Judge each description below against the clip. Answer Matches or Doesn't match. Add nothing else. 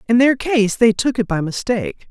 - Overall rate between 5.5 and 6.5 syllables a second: Doesn't match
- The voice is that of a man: Doesn't match